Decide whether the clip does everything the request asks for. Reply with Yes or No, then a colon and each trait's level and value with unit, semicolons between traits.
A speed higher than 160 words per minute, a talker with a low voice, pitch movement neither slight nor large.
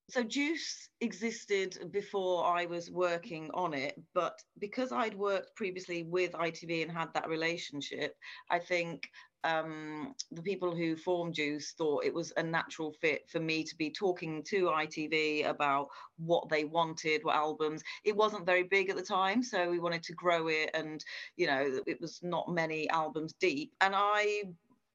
No: average, 170 wpm; medium, 170 Hz; average, 3.7 semitones